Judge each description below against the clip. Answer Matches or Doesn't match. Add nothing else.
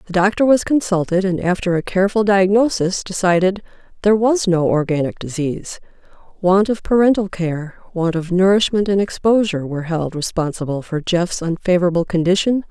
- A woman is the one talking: Matches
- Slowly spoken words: Doesn't match